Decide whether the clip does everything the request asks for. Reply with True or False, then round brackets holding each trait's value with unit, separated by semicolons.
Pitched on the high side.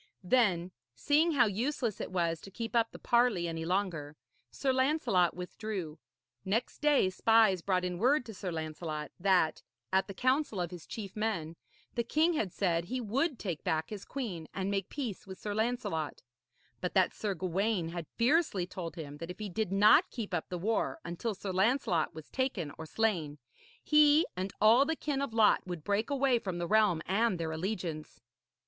True (195 Hz)